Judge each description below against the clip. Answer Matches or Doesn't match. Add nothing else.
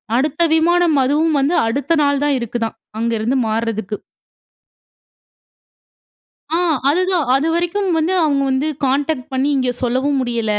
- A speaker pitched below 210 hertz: Doesn't match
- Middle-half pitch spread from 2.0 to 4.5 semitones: Doesn't match